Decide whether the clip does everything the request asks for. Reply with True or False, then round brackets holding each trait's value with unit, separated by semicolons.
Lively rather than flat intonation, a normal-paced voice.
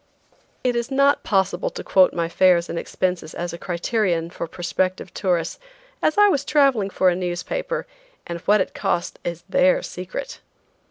True (7.7 semitones; 165 wpm)